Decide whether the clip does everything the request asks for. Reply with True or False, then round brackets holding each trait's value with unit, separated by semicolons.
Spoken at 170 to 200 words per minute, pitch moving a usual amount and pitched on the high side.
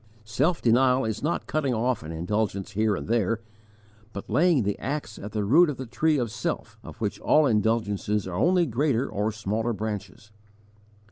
False (180 wpm; 4.3 semitones; 110 Hz)